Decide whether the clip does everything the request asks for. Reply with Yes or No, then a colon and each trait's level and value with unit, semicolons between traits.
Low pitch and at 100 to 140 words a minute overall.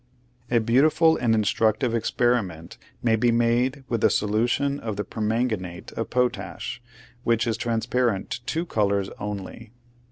Yes: low, 115 Hz; slow, 135 wpm